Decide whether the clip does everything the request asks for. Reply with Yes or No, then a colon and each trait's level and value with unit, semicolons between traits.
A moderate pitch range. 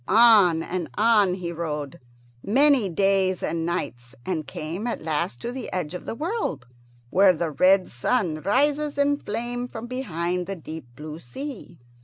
No: wide, 6.7 semitones